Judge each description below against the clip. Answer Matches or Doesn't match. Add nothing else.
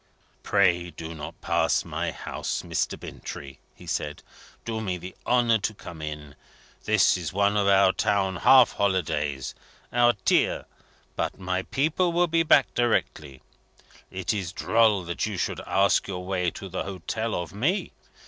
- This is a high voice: Doesn't match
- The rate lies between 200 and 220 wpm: Doesn't match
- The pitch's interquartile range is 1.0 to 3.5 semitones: Doesn't match